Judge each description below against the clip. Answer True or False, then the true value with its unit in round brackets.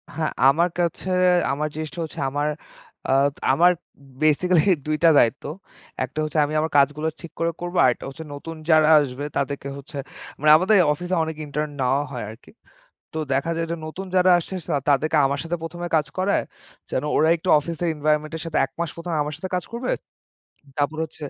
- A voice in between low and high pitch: True (155 Hz)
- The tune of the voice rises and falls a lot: False (2.7 semitones)